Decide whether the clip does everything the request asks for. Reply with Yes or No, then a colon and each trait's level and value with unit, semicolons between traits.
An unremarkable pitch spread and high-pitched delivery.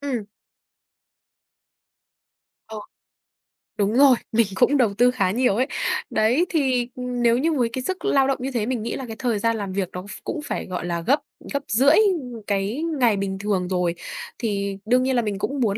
Yes: average, 4.5 semitones; high, 235 Hz